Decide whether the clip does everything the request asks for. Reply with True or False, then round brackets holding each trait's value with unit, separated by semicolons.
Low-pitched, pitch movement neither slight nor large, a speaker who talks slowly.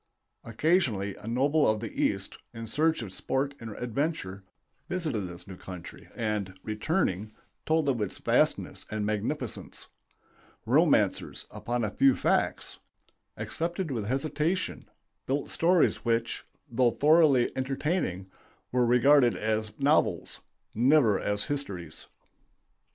False (120 Hz; 5.7 semitones; 120 wpm)